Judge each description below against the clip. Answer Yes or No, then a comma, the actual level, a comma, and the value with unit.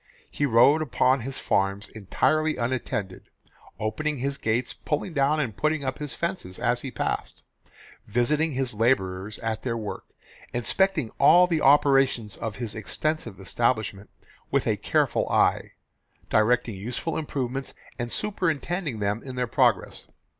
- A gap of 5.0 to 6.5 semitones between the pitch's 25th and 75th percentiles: Yes, average, 5.3 semitones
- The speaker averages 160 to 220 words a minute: No, average, 140 wpm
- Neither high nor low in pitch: No, low, 125 Hz